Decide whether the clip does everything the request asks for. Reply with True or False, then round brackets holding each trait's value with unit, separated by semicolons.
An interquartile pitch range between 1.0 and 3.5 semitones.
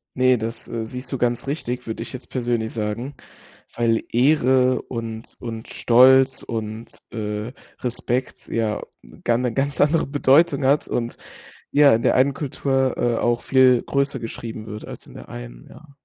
True (2.7 semitones)